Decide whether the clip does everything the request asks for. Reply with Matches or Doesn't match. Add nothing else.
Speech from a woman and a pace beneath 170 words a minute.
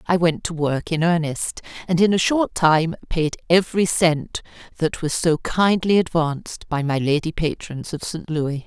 Doesn't match